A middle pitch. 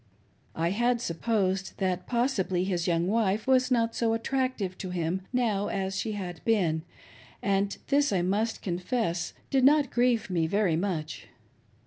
No: high, 200 Hz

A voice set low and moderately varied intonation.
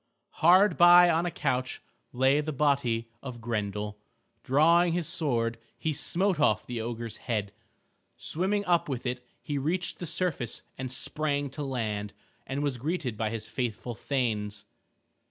No: low, 130 Hz; wide, 5.7 semitones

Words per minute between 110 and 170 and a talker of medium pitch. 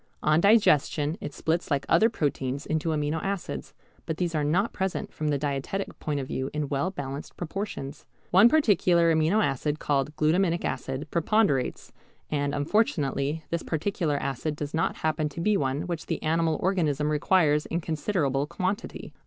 Yes: average, 160 wpm; medium, 155 Hz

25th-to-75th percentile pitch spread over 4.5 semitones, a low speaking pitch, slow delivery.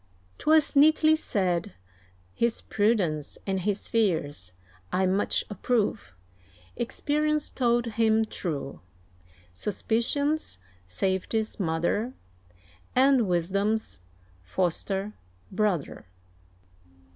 No: average, 5.2 semitones; high, 210 Hz; slow, 75 wpm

